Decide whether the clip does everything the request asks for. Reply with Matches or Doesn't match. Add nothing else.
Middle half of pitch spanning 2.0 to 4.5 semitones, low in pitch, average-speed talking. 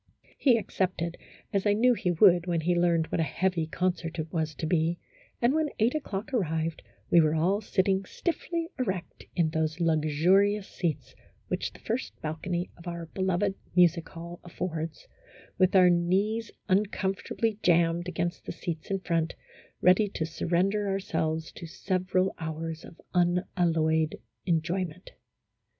Doesn't match